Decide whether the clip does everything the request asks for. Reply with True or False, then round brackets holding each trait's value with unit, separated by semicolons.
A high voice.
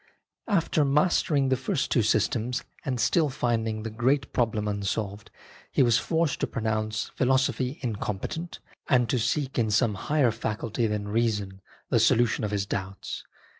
False (115 Hz)